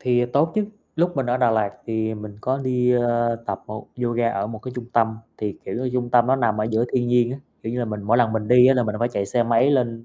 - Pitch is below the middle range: Yes, low, 120 Hz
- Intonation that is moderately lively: No, narrow, 2.1 semitones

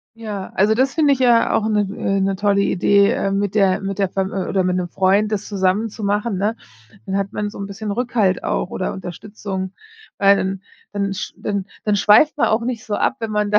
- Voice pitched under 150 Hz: No, high, 200 Hz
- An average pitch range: No, narrow, 1.8 semitones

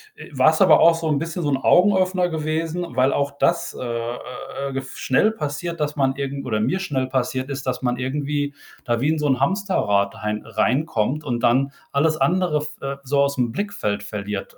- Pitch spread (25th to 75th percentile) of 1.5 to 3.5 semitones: No, average, 4.1 semitones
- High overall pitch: No, medium, 140 Hz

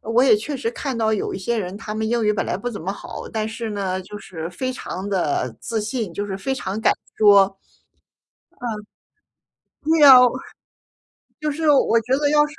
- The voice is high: Yes, high, 220 Hz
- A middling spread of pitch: Yes, average, 4.5 semitones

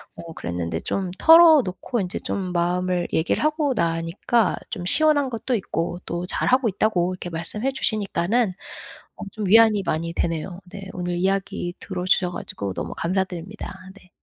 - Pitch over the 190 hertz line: No, medium, 185 Hz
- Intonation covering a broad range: No, average, 4.2 semitones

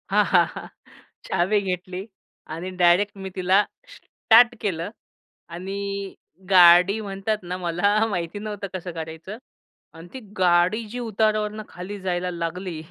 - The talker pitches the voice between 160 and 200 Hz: Yes, high, 190 Hz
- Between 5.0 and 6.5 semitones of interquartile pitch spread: No, average, 2.8 semitones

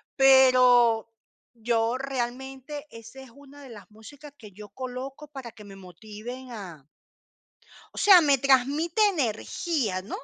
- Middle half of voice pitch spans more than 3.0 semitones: Yes, average, 3.6 semitones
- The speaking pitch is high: Yes, very high, 255 Hz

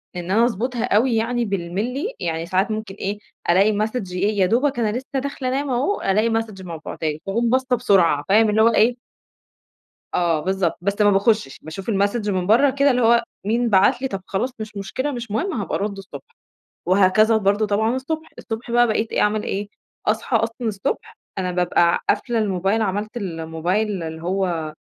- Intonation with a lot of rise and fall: No, average, 3.8 semitones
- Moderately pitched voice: No, high, 210 Hz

